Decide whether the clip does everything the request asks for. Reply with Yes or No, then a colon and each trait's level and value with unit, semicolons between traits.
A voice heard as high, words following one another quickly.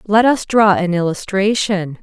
No: high, 195 Hz; average, 150 wpm